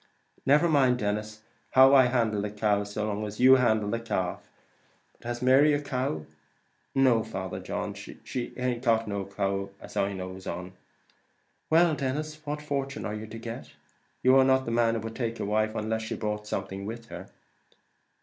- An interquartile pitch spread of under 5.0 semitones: Yes, average, 3.9 semitones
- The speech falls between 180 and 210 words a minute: Yes, average, 190 wpm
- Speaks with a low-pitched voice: Yes, low, 115 Hz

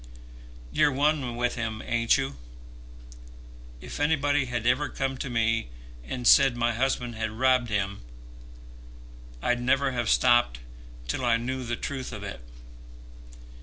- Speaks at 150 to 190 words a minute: No, slow, 135 wpm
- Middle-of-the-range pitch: No, low, 120 Hz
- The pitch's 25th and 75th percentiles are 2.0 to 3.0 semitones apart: Yes, average, 2.7 semitones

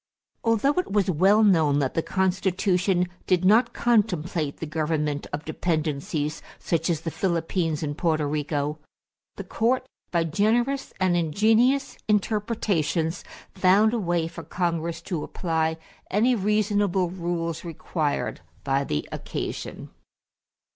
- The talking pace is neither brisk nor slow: No, slow, 125 wpm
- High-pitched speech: No, medium, 175 Hz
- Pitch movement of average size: Yes, average, 4.5 semitones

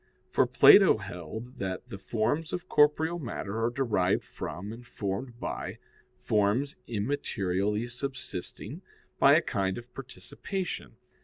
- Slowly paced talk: Yes, slow, 125 wpm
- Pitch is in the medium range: No, low, 115 Hz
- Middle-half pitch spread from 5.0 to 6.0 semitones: Yes, average, 5.3 semitones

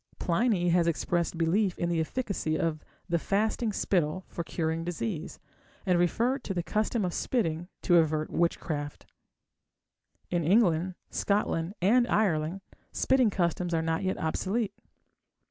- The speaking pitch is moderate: Yes, medium, 175 Hz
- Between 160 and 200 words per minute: No, slow, 135 wpm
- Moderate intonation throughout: Yes, average, 3.8 semitones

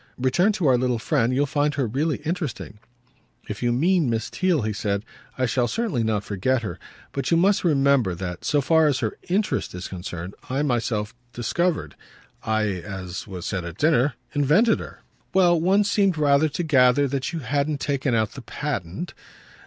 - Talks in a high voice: No, low, 135 Hz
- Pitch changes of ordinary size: No, wide, 6.4 semitones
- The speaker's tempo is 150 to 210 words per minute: Yes, average, 180 wpm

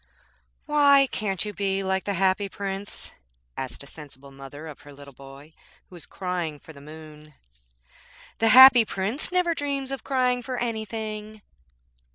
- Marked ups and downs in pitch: Yes, wide, 7.9 semitones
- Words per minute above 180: No, average, 155 wpm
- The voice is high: Yes, high, 195 Hz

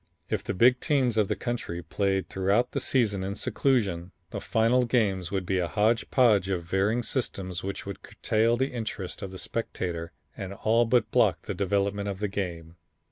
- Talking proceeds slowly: No, average, 190 wpm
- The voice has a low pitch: Yes, low, 100 Hz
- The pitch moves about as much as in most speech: Yes, average, 3.7 semitones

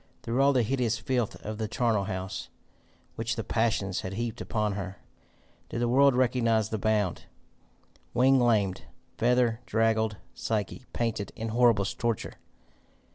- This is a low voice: Yes, low, 115 Hz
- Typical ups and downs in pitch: No, narrow, 2.3 semitones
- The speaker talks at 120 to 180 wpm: Yes, average, 140 wpm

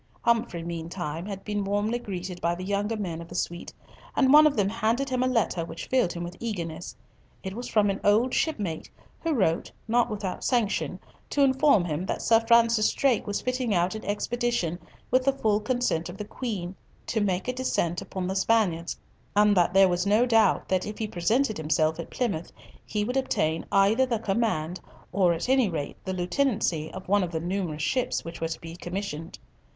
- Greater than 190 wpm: Yes, average, 200 wpm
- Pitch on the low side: No, high, 200 Hz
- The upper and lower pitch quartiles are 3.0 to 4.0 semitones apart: No, average, 5.1 semitones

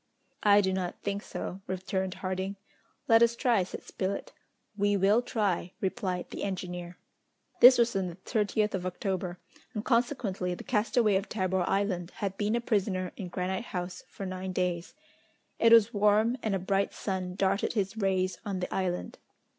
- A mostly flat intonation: Yes, narrow, 2.2 semitones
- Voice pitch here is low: No, high, 195 Hz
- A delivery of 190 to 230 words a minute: No, average, 170 wpm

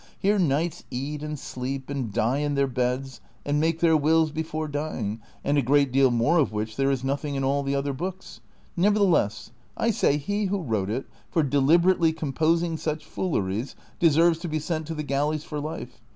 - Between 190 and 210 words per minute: Yes, average, 195 wpm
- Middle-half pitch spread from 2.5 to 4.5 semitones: Yes, average, 3.3 semitones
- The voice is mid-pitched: Yes, medium, 145 Hz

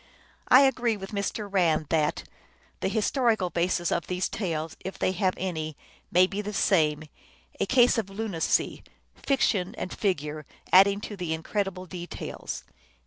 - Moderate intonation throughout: Yes, average, 3.5 semitones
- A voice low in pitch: No, high, 190 Hz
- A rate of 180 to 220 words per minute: No, average, 150 wpm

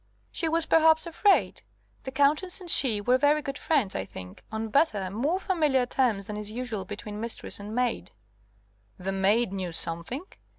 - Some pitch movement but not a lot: No, wide, 6.7 semitones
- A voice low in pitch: No, high, 245 Hz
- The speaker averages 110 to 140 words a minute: No, average, 170 wpm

